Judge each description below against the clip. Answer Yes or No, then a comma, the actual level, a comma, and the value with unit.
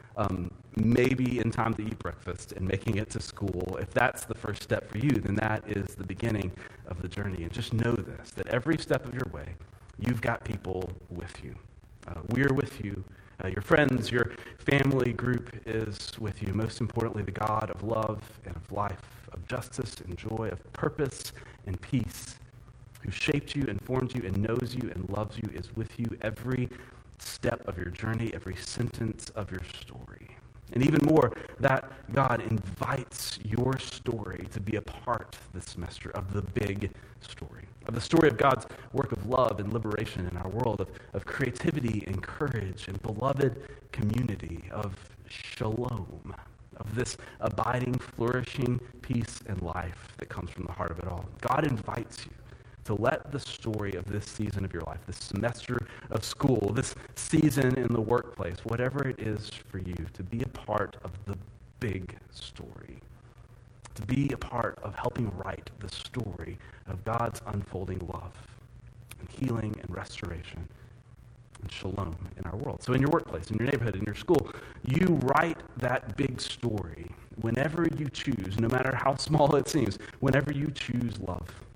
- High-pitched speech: No, low, 115 Hz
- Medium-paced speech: Yes, average, 175 wpm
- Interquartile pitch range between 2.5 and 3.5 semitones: No, average, 3.9 semitones